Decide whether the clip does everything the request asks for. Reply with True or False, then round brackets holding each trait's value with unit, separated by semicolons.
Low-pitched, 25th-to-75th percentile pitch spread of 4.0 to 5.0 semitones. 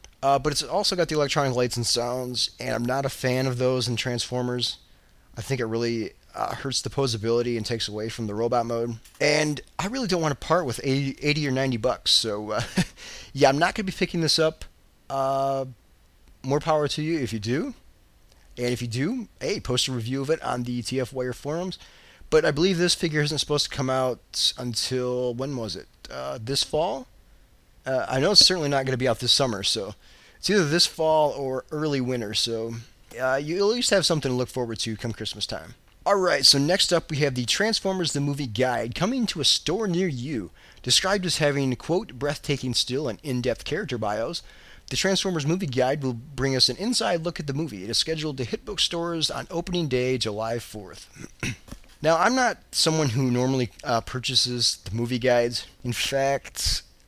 True (130 Hz; 4.5 semitones)